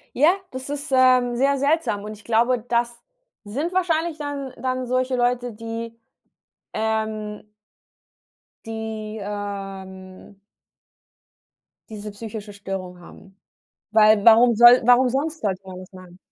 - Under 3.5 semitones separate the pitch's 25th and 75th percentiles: No, average, 3.8 semitones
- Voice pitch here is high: Yes, high, 230 Hz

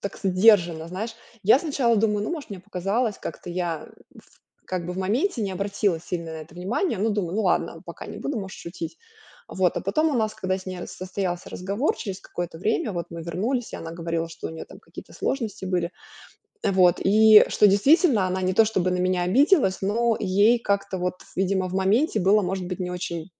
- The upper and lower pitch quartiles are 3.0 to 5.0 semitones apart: Yes, average, 3.3 semitones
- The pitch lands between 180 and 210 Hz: Yes, high, 190 Hz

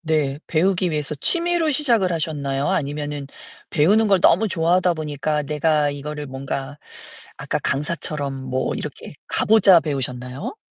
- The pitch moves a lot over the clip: No, average, 4.4 semitones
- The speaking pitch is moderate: Yes, medium, 150 Hz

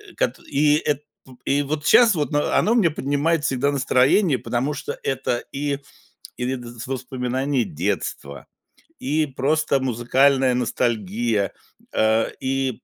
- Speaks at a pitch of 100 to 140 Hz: Yes, low, 135 Hz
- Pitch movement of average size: Yes, average, 3.1 semitones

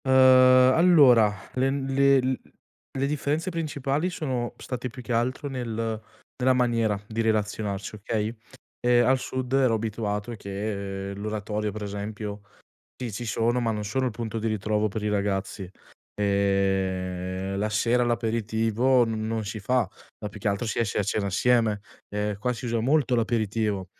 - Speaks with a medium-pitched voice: No, low, 110 Hz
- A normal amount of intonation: Yes, average, 3.2 semitones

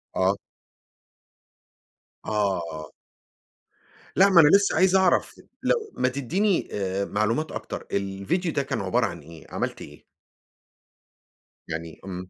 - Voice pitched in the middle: No, low, 105 Hz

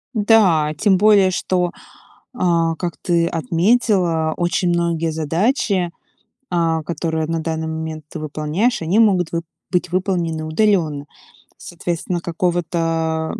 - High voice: No, medium, 170 Hz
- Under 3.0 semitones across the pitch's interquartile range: Yes, narrow, 2.5 semitones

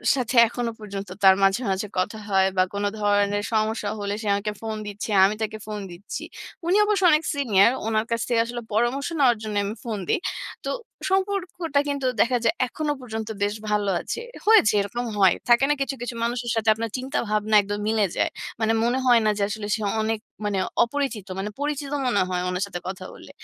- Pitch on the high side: Yes, high, 220 Hz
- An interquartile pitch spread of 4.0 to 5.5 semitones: No, average, 3.2 semitones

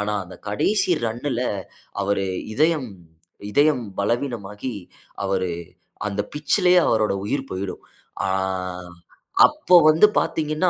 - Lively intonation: Yes, wide, 6.9 semitones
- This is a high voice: No, low, 120 Hz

